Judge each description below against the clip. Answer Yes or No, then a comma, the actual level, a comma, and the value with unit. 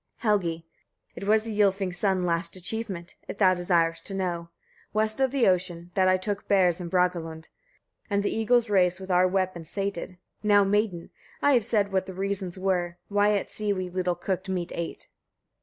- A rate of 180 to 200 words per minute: Yes, average, 190 wpm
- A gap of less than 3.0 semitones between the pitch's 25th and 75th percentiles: Yes, narrow, 2.5 semitones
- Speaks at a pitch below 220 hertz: Yes, high, 190 Hz